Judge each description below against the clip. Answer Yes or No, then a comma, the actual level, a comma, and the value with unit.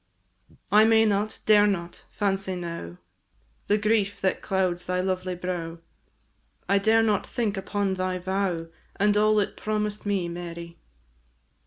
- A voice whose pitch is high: Yes, high, 195 Hz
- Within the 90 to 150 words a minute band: Yes, average, 140 wpm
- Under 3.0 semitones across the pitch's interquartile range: Yes, narrow, 2.5 semitones